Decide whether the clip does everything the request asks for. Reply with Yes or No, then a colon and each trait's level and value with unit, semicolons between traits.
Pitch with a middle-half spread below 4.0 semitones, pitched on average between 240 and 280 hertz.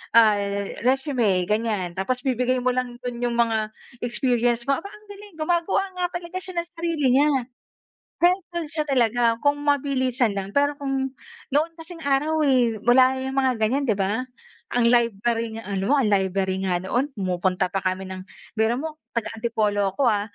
No: average, 5.1 semitones; high, 245 Hz